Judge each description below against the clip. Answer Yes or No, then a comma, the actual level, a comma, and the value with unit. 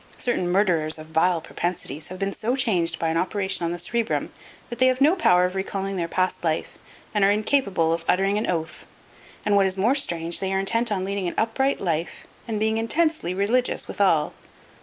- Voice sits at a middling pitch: No, high, 195 Hz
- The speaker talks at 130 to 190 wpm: No, average, 200 wpm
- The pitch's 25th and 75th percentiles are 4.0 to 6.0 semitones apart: Yes, average, 4.3 semitones